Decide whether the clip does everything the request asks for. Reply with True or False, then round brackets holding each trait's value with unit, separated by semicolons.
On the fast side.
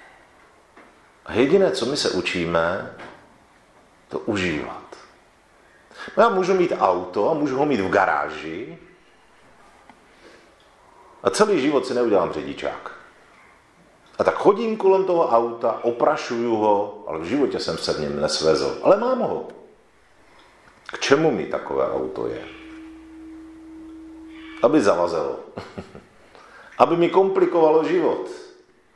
False (115 wpm)